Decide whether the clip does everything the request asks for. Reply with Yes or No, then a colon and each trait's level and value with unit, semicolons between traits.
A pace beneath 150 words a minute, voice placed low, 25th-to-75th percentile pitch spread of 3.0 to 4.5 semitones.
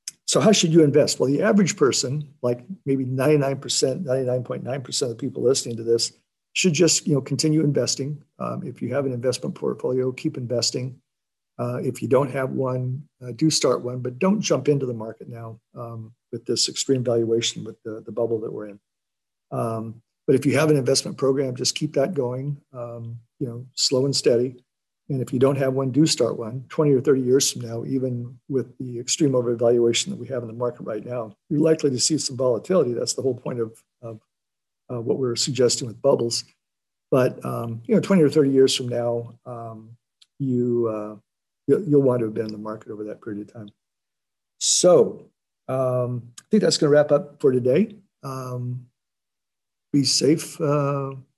No: average, 195 wpm; low, 130 Hz; average, 3.3 semitones